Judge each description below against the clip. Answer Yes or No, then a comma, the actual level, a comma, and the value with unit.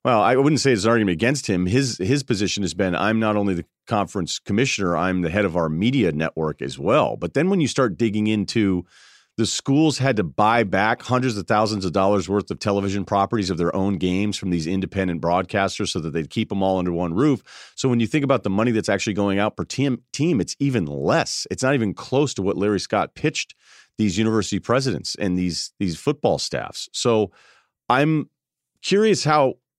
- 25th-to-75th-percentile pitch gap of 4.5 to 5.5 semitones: Yes, average, 5.1 semitones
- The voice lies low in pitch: Yes, low, 105 Hz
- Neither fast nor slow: No, fast, 215 wpm